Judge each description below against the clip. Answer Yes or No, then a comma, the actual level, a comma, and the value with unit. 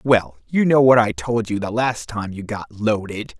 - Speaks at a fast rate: Yes, fast, 230 wpm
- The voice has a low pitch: Yes, low, 115 Hz